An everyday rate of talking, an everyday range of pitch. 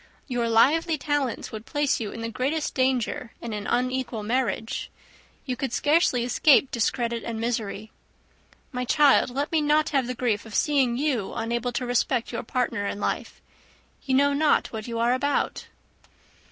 Yes: average, 165 wpm; average, 3.5 semitones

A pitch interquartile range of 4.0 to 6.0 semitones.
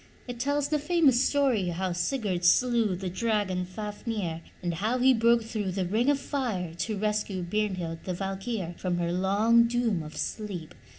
Yes: average, 4.7 semitones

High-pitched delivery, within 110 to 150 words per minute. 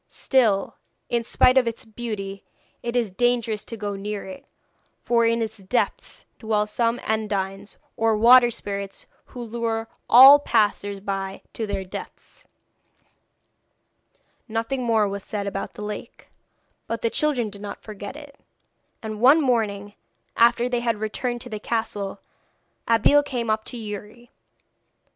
Yes: high, 225 Hz; average, 145 wpm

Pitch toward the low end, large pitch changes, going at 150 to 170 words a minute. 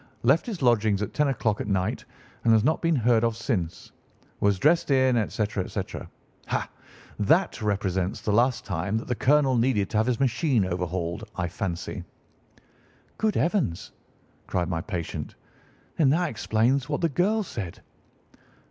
Yes: low, 115 Hz; wide, 5.8 semitones; average, 155 wpm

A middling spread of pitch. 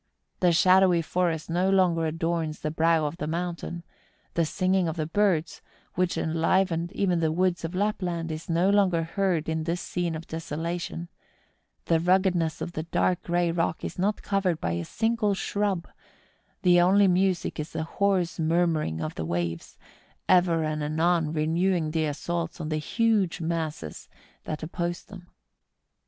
No: narrow, 2.3 semitones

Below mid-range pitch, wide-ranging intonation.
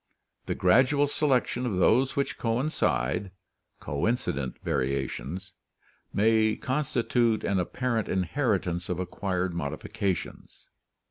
Yes: low, 100 Hz; wide, 5.8 semitones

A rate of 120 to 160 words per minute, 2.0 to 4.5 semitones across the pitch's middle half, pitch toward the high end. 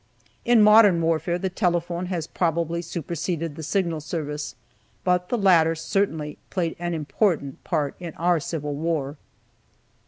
No: slow, 135 wpm; narrow, 2.5 semitones; medium, 170 Hz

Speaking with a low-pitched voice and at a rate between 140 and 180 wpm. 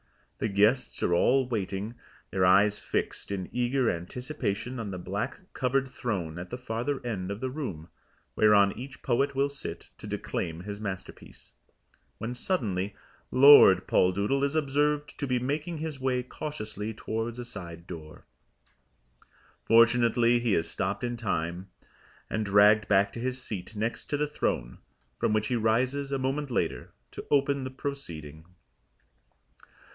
Yes: low, 115 Hz; average, 150 wpm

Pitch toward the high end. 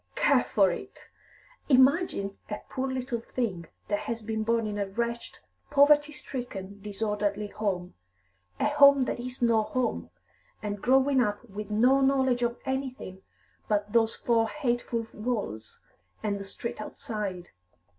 Yes: high, 230 Hz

